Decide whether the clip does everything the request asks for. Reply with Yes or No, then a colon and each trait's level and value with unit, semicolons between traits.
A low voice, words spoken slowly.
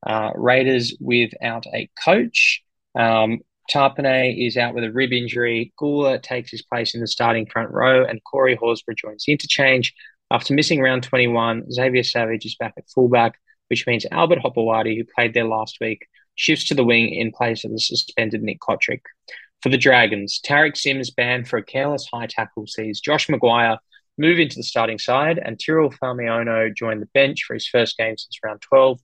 No: low, 120 Hz; average, 185 wpm